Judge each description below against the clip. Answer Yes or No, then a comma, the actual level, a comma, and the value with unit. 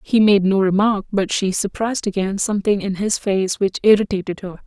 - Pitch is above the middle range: Yes, high, 200 Hz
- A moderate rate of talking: Yes, average, 195 wpm